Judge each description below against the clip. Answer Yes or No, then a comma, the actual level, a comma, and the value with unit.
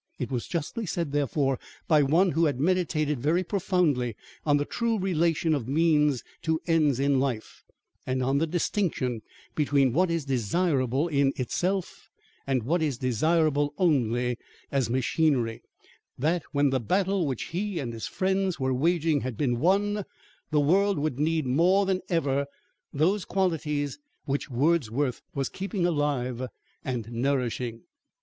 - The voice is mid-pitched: Yes, medium, 145 Hz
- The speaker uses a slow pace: No, average, 145 wpm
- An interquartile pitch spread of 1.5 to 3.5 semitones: No, average, 4.7 semitones